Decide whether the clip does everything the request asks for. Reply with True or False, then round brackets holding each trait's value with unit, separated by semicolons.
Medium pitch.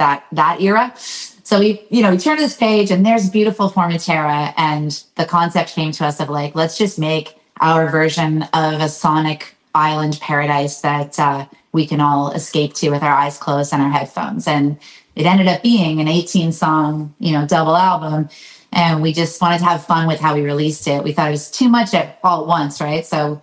True (160 Hz)